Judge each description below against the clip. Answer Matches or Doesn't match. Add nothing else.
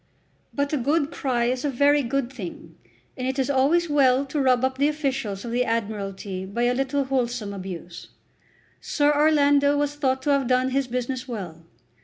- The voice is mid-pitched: Doesn't match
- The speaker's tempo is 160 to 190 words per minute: Matches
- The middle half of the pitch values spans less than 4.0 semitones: Matches